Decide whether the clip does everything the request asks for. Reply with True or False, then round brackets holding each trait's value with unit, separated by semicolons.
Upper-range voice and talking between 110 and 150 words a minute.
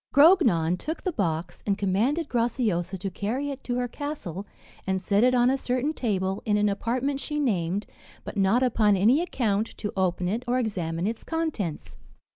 False (220 Hz; 180 wpm)